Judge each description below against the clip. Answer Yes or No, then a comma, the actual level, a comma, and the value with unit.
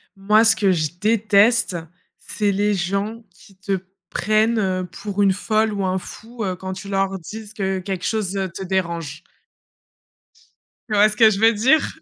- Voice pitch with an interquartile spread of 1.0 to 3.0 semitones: Yes, narrow, 2.4 semitones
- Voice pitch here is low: No, high, 200 Hz